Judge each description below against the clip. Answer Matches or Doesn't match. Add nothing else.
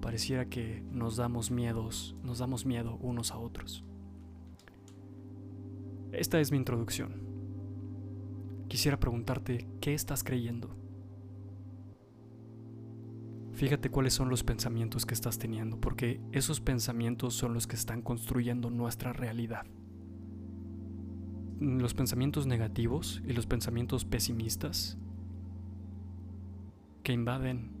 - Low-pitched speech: Matches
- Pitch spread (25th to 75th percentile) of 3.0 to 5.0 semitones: Matches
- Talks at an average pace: Doesn't match